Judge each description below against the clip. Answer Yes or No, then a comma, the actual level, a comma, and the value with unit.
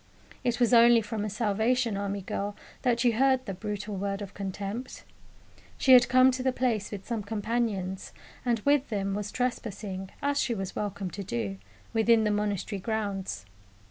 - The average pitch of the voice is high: Yes, high, 210 Hz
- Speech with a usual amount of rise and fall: Yes, average, 3.3 semitones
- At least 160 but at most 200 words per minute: Yes, average, 175 wpm